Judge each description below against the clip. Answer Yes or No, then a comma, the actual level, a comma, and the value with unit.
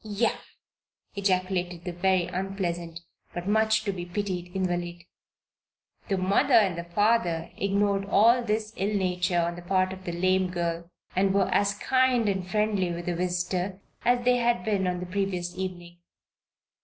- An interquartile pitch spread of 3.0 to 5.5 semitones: No, narrow, 2.6 semitones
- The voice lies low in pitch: No, medium, 185 Hz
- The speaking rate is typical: Yes, average, 155 wpm